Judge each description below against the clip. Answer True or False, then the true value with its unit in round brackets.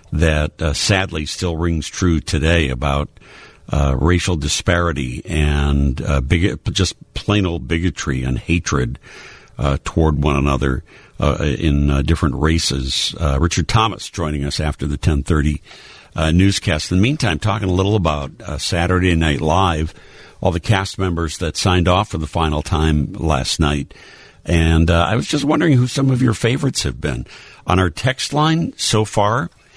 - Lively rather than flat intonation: False (4.5 semitones)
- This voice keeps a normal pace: True (165 wpm)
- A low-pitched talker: True (85 Hz)